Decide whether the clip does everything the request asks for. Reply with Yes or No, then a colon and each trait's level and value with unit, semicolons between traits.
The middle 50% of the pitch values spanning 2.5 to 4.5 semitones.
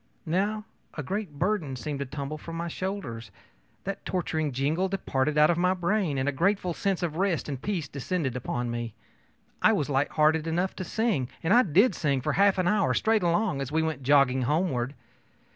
No: wide, 5.5 semitones